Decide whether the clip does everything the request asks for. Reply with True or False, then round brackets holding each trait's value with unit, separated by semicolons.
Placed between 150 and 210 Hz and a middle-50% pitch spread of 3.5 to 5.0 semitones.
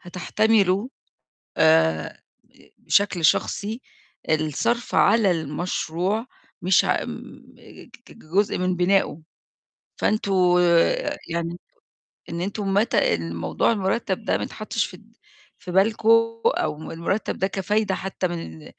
True (185 Hz; 3.9 semitones)